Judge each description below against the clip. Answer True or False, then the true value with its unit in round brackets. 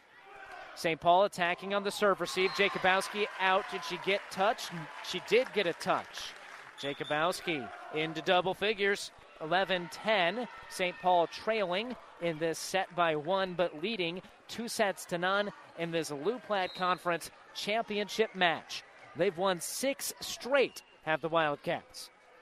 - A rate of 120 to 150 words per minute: True (135 wpm)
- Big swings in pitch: False (3.2 semitones)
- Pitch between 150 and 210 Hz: True (185 Hz)